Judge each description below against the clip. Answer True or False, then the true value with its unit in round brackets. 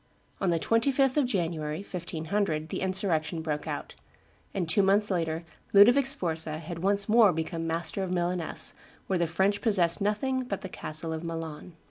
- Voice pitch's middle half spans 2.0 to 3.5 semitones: False (3.9 semitones)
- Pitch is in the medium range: True (180 Hz)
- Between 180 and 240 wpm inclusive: False (165 wpm)